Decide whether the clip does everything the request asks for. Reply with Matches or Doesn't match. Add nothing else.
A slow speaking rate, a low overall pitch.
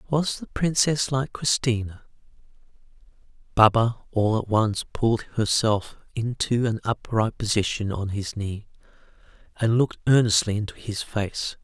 Matches